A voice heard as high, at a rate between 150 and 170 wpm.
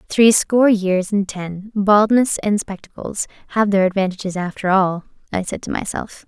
Yes: high, 200 Hz; average, 165 wpm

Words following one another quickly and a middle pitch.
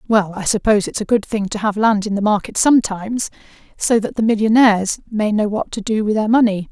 No: fast, 230 wpm; high, 210 Hz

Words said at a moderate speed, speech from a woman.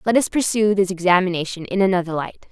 Yes: average, 190 wpm; female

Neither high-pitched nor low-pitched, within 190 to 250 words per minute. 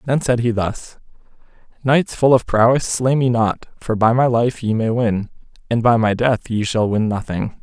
No: low, 115 Hz; fast, 205 wpm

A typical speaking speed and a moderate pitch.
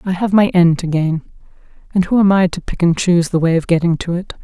No: fast, 255 wpm; medium, 175 Hz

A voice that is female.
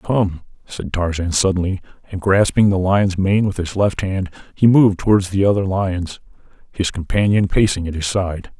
No: male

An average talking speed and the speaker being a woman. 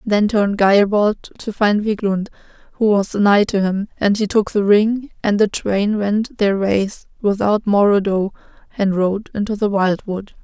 Yes: average, 180 wpm; female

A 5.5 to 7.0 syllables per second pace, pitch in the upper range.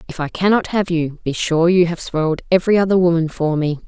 No: 6.0 syllables/s; medium, 170 Hz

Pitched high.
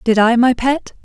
Yes: high, 245 Hz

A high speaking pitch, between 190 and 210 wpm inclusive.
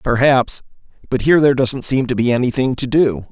No: low, 130 Hz; average, 200 wpm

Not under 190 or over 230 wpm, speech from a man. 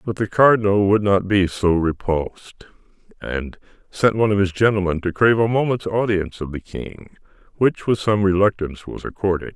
No: average, 175 wpm; male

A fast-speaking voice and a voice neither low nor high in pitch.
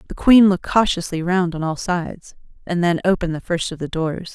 Yes: fast, 220 wpm; medium, 175 Hz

